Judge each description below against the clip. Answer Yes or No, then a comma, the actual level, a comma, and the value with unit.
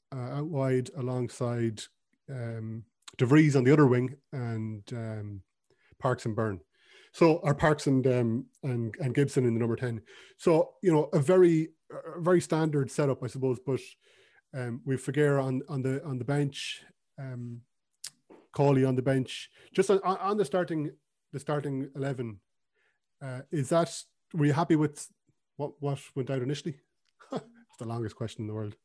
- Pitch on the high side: No, low, 135 Hz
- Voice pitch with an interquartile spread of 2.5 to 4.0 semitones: Yes, average, 3.6 semitones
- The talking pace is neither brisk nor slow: Yes, average, 165 wpm